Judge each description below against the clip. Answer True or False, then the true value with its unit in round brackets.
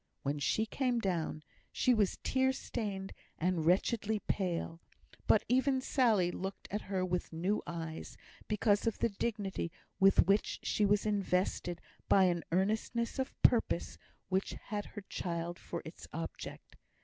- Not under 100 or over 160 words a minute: True (145 wpm)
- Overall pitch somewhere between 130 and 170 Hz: False (195 Hz)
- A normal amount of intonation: True (3.8 semitones)